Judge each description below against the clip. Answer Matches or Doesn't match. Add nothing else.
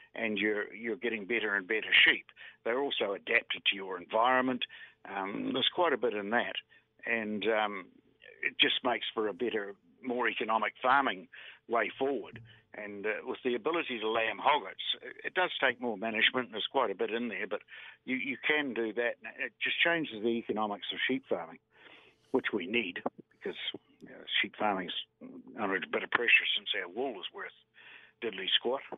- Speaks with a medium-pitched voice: Doesn't match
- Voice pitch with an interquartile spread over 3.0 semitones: Matches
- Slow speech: Doesn't match